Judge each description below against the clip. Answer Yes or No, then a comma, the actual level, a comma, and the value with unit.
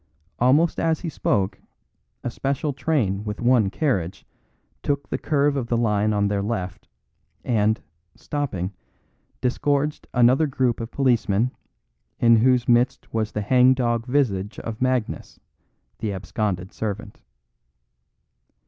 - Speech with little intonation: No, average, 4.1 semitones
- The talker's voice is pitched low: Yes, low, 120 Hz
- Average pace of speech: No, slow, 120 wpm